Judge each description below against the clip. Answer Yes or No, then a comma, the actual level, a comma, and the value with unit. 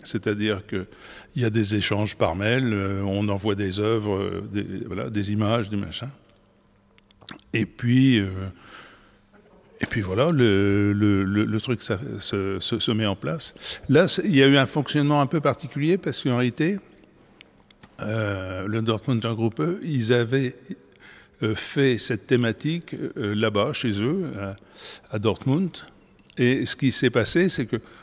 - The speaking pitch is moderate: No, low, 115 Hz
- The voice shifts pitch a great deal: No, average, 4.5 semitones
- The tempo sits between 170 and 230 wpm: No, average, 155 wpm